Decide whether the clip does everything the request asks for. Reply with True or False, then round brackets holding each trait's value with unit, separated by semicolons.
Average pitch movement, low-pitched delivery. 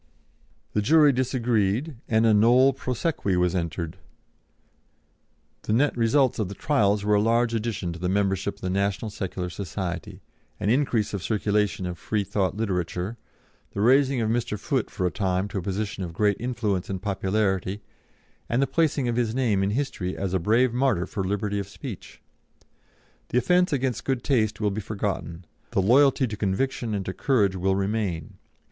True (4.1 semitones; 105 Hz)